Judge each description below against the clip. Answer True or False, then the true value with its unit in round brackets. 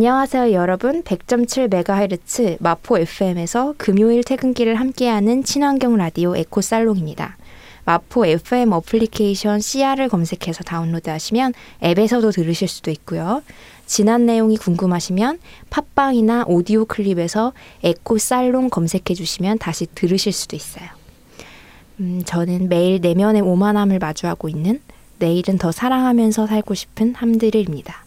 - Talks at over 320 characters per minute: True (330 characters per minute)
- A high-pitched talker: True (210 Hz)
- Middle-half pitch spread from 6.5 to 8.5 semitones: False (5.2 semitones)